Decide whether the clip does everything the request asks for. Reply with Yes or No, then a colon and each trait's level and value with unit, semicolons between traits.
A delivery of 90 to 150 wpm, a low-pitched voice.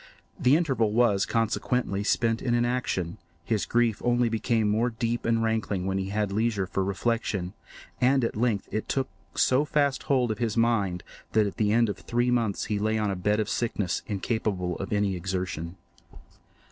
No: average, 180 wpm; low, 110 Hz